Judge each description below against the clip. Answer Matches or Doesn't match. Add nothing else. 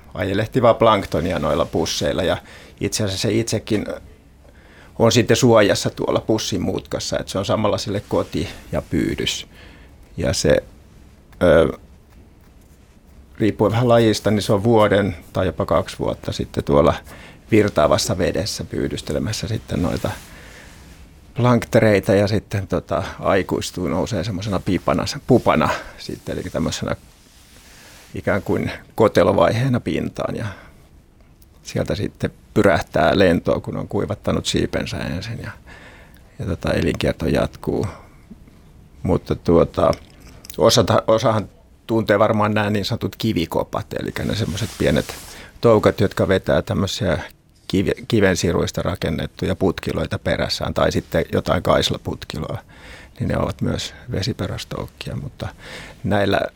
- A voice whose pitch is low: Matches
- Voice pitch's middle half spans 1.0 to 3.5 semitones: Doesn't match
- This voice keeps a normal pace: Matches